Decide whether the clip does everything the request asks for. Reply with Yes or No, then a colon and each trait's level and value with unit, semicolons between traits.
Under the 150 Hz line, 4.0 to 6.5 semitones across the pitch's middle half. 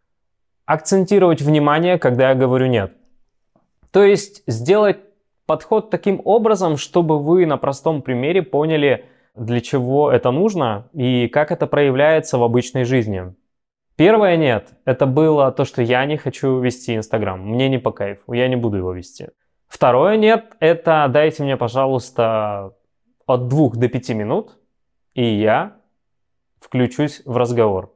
Yes: low, 135 Hz; average, 4.7 semitones